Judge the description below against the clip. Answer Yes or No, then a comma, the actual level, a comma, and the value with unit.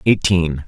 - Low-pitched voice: Yes, very low, 85 Hz